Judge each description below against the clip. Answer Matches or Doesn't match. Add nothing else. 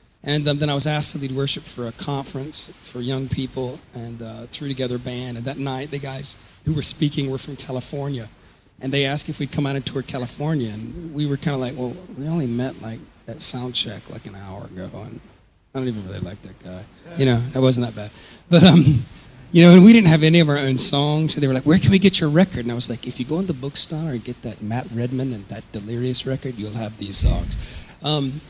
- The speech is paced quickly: Matches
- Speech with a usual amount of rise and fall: Matches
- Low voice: Matches